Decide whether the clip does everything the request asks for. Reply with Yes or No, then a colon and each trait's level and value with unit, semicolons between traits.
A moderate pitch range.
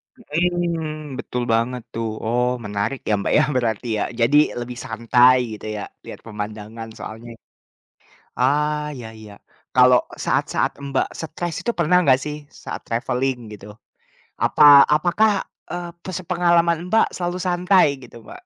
No: wide, 6.6 semitones